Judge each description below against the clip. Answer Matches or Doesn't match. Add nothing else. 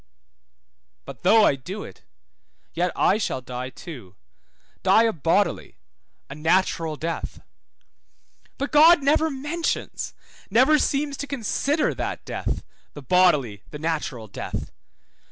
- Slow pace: Matches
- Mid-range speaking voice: Matches